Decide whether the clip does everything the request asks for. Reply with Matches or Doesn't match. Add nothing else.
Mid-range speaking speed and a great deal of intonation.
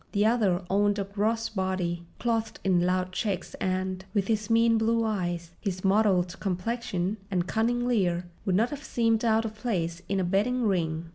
Doesn't match